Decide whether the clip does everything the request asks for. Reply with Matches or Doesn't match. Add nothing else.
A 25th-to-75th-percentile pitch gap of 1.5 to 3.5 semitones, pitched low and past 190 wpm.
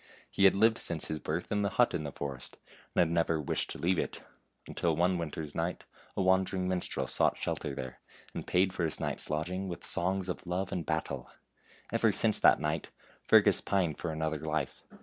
Matches